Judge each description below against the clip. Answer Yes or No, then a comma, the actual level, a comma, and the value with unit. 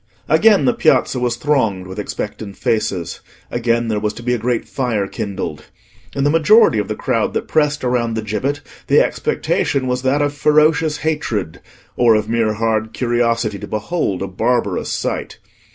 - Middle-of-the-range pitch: No, low, 115 Hz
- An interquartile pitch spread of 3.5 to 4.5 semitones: No, average, 5.1 semitones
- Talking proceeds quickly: No, average, 170 wpm